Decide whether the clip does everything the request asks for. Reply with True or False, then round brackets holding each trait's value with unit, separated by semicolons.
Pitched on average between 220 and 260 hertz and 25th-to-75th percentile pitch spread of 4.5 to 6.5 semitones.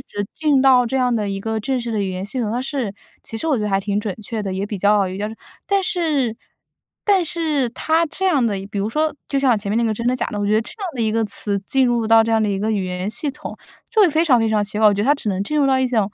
True (225 Hz; 4.8 semitones)